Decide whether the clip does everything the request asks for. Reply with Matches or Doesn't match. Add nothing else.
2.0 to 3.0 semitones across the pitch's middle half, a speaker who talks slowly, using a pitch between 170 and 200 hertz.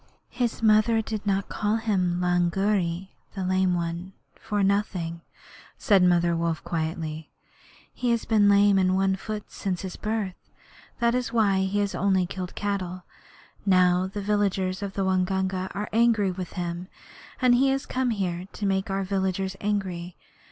Doesn't match